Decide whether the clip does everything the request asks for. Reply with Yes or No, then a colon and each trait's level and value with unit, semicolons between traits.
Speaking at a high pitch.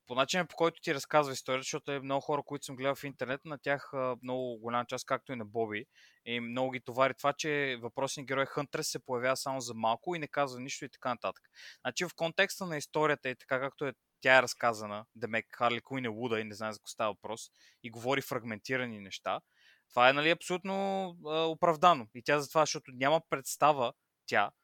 No: low, 135 Hz